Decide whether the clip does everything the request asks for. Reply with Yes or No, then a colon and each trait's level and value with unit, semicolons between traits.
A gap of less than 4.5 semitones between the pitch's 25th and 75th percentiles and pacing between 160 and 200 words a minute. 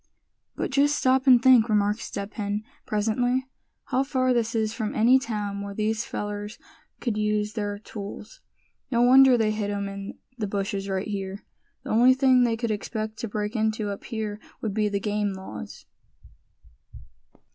Yes: average, 2.8 semitones; average, 170 wpm